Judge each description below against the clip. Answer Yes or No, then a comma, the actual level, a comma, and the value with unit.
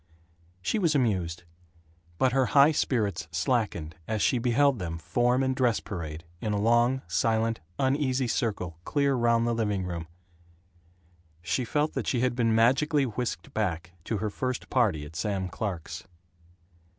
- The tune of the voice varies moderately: No, wide, 5.9 semitones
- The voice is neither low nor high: No, low, 115 Hz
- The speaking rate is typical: Yes, average, 150 wpm